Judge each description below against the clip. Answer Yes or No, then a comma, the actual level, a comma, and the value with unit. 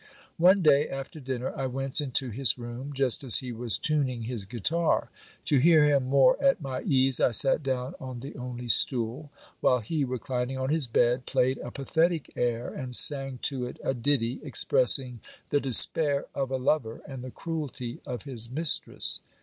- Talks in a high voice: No, low, 130 Hz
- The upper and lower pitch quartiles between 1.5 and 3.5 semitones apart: Yes, narrow, 2.6 semitones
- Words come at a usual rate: Yes, average, 180 wpm